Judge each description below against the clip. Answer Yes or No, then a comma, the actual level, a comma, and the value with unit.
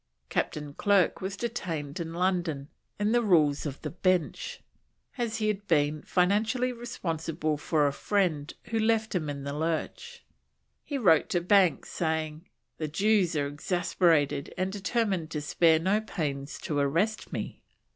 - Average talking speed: Yes, average, 150 wpm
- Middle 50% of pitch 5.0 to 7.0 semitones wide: Yes, average, 5.3 semitones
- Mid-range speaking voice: Yes, medium, 175 Hz